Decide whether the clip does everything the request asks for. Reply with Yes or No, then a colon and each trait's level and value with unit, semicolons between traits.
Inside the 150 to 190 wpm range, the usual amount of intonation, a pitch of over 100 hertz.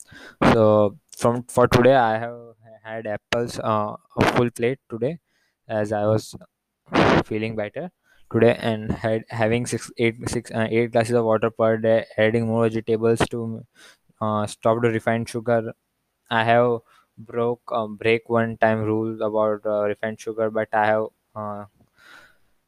No: average, 155 wpm; narrow, 1.3 semitones; low, 115 Hz